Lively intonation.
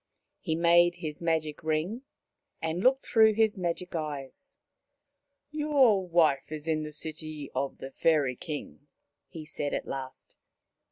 No: average, 4.1 semitones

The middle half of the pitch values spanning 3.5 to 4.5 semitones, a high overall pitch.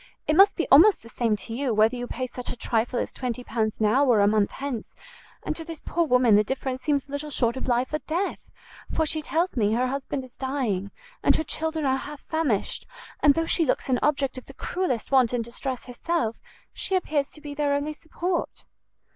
Yes: average, 4.2 semitones; very high, 265 Hz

